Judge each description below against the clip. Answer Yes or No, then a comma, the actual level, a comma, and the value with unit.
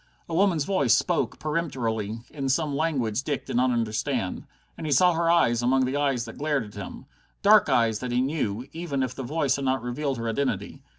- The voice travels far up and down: No, average, 4.2 semitones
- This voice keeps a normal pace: No, fast, 210 wpm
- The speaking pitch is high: No, low, 135 Hz